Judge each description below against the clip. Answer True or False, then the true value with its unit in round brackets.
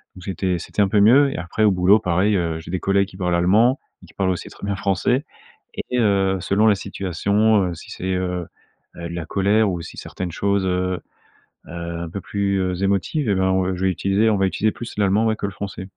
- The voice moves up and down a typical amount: False (2.1 semitones)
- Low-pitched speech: True (95 Hz)